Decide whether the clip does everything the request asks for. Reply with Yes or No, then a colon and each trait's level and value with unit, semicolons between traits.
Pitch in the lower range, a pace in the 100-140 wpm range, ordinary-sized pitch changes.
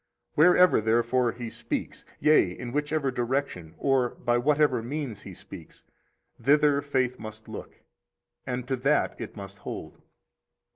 Yes: low, 125 Hz; slow, 135 wpm; average, 3.9 semitones